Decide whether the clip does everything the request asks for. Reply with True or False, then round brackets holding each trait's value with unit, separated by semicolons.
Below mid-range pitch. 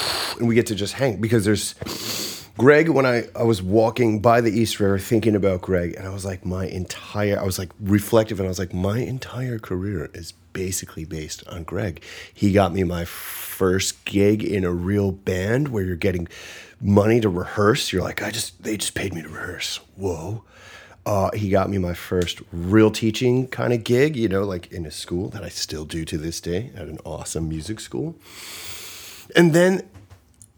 True (100 Hz)